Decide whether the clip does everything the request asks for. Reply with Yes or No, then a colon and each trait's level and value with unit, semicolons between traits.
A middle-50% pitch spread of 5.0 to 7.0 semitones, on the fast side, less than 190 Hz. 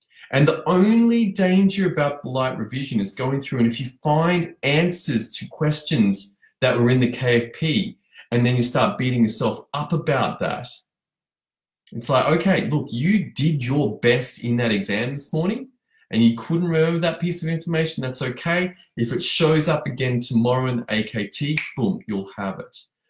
No: wide, 5.5 semitones; average, 175 wpm; medium, 140 Hz